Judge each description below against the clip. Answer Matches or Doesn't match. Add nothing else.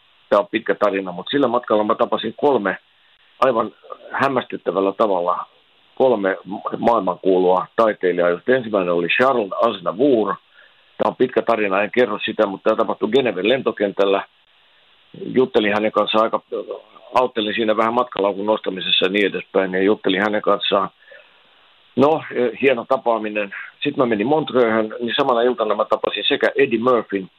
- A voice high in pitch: Doesn't match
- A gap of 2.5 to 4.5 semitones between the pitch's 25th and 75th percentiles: Matches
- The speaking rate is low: Doesn't match